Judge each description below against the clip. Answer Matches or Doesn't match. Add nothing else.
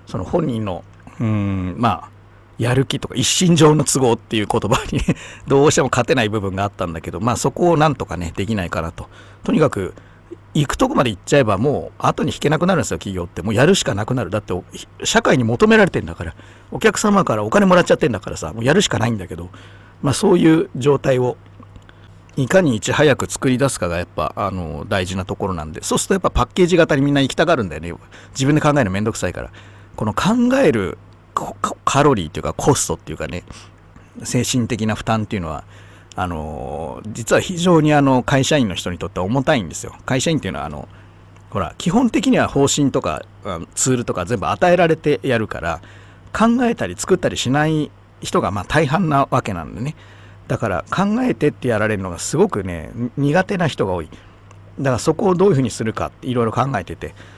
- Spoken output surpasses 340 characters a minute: Matches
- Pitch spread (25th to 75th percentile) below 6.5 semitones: Doesn't match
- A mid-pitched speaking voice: Doesn't match